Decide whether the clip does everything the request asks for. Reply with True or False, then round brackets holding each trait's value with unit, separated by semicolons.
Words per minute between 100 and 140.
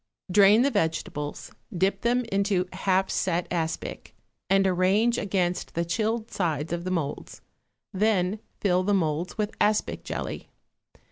True (135 wpm)